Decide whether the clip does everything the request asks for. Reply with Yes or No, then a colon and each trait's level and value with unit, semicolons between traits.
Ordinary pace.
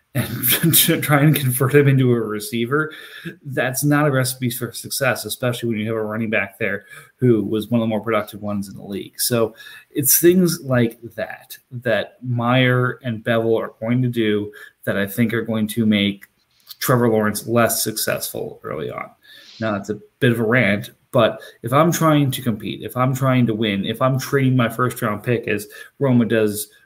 Yes: average, 195 wpm